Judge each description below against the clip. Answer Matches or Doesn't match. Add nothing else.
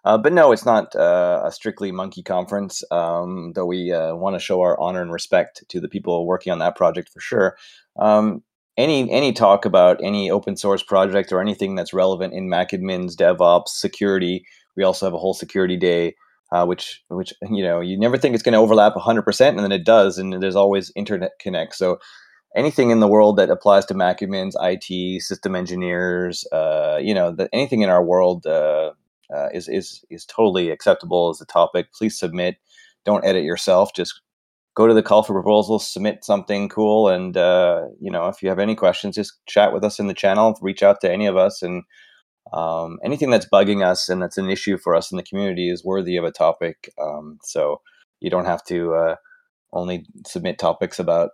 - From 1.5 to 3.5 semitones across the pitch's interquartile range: Matches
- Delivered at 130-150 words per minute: Doesn't match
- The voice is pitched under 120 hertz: Matches